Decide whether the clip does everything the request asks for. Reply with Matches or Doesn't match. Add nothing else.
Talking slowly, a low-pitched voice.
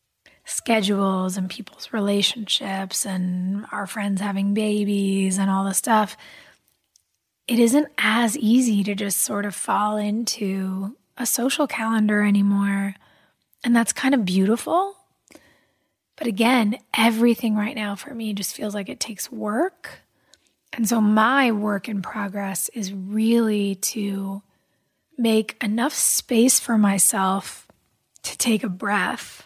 Doesn't match